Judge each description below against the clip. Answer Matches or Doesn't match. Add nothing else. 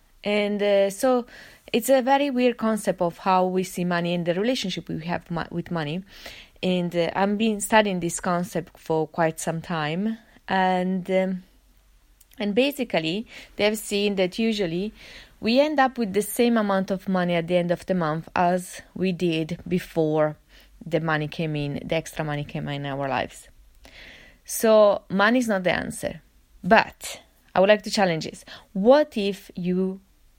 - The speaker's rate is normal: Matches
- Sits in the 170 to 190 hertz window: Matches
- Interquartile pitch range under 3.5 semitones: Doesn't match